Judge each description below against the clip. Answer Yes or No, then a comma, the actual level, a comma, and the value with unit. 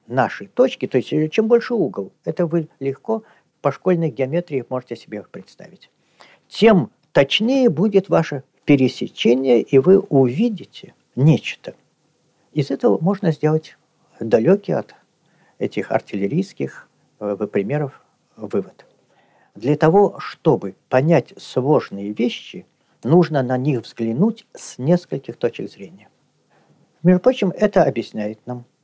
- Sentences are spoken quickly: No, slow, 110 wpm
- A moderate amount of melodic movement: No, wide, 6.8 semitones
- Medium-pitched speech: Yes, medium, 155 Hz